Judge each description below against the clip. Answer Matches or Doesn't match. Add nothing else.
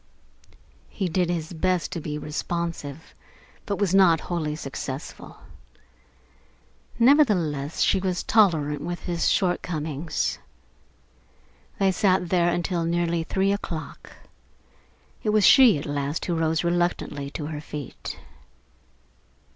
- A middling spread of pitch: Matches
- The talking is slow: Matches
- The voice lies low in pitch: Doesn't match